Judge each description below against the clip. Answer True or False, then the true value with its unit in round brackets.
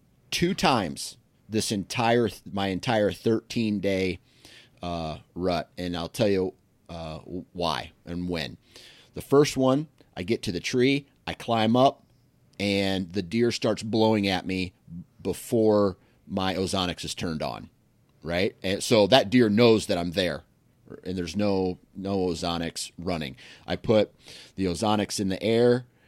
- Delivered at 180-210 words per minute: False (145 wpm)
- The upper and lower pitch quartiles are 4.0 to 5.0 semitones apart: True (4.7 semitones)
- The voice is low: True (100 Hz)